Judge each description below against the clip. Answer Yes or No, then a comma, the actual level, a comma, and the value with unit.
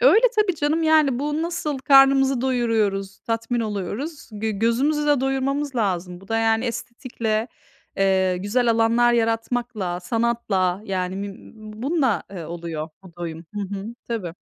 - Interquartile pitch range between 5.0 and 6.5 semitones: Yes, wide, 5.5 semitones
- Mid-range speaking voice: No, high, 225 Hz